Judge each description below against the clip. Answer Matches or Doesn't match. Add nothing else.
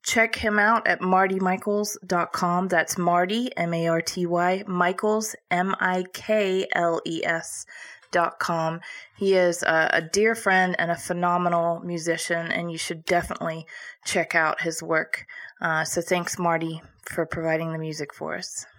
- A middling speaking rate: Doesn't match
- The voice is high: Doesn't match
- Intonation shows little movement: Matches